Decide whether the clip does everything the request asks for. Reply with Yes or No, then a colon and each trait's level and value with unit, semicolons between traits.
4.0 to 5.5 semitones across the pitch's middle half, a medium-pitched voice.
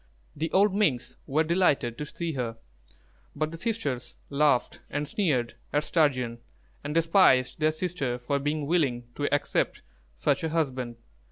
Yes: average, 4.3 semitones; medium, 145 Hz